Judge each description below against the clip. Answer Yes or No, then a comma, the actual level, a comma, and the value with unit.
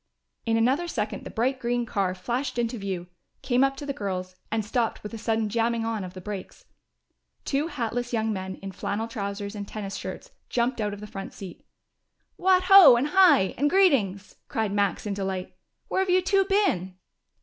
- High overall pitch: Yes, high, 225 Hz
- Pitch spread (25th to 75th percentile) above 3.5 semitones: Yes, average, 5.2 semitones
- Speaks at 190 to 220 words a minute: Yes, average, 195 wpm